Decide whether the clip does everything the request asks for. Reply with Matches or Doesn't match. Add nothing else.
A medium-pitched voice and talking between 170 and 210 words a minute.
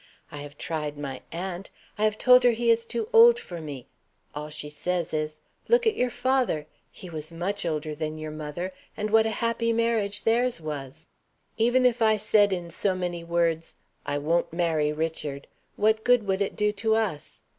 Matches